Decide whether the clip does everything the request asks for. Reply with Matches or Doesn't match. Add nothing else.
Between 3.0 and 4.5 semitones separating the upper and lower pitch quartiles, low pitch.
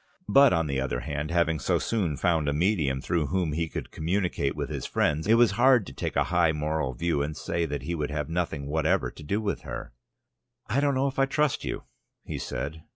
Doesn't match